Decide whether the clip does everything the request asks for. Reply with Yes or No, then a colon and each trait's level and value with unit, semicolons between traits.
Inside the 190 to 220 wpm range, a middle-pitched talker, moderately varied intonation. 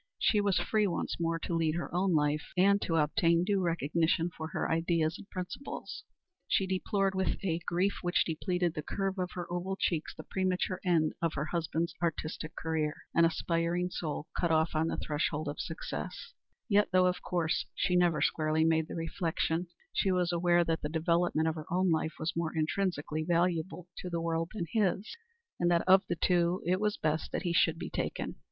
No: average, 195 wpm; medium, 170 Hz; narrow, 2.1 semitones